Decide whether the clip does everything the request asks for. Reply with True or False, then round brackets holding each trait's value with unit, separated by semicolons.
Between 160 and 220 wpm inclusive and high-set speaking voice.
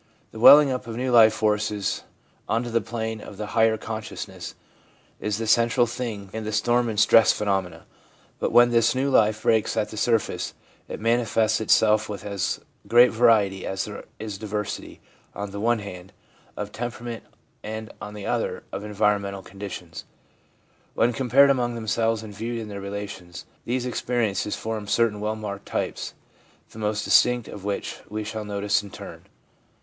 False (170 wpm; 110 Hz)